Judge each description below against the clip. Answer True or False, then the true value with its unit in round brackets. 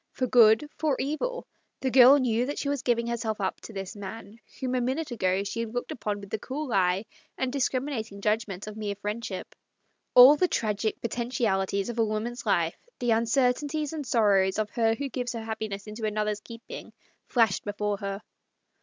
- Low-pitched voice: False (225 Hz)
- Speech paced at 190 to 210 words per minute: True (200 wpm)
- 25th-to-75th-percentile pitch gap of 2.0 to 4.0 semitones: True (3.5 semitones)